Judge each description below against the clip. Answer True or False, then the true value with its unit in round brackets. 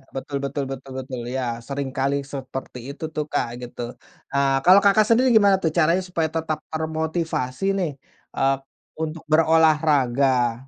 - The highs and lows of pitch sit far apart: False (3.4 semitones)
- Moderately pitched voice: True (150 Hz)